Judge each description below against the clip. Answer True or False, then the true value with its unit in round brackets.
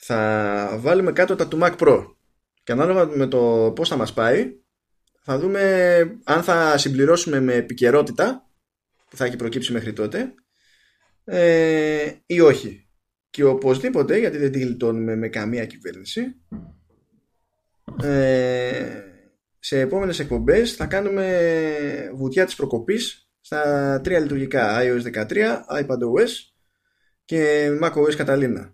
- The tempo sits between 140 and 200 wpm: False (115 wpm)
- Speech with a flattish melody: False (5.9 semitones)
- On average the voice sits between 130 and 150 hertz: True (140 Hz)